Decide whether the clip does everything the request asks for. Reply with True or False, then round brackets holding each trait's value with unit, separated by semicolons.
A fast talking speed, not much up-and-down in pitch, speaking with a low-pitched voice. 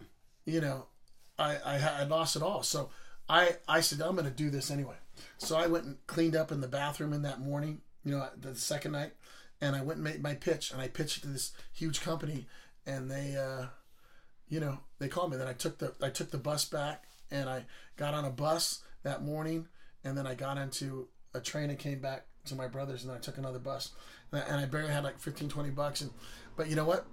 False (235 wpm; 2.3 semitones; 145 Hz)